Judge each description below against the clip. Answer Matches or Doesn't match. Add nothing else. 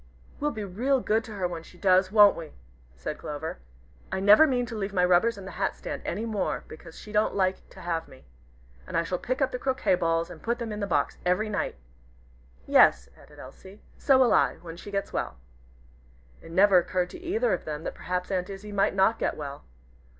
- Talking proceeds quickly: Matches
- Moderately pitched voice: Doesn't match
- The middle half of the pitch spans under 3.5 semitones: Doesn't match